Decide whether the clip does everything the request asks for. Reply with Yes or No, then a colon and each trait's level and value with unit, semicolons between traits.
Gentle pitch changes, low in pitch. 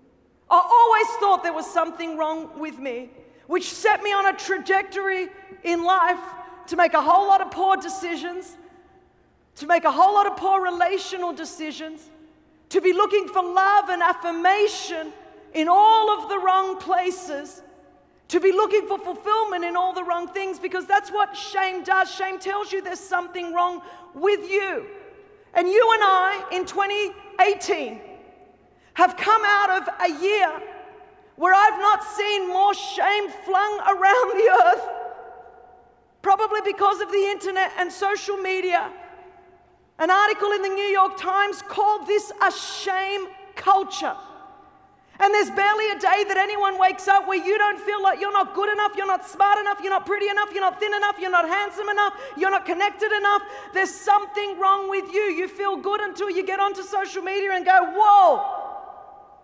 No: narrow, 1.7 semitones; very high, 385 Hz